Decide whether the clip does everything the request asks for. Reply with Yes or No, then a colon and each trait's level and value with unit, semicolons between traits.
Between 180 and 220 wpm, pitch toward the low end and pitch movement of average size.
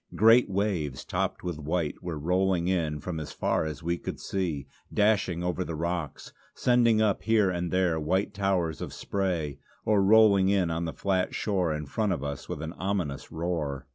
Yes: average, 185 wpm; very low, 90 Hz; average, 3.7 semitones